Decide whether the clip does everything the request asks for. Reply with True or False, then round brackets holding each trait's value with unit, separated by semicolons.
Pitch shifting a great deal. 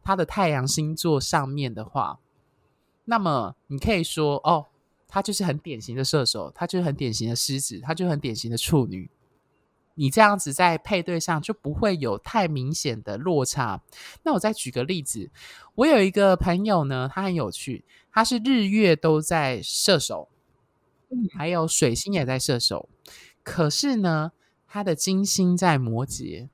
True (5.9 semitones)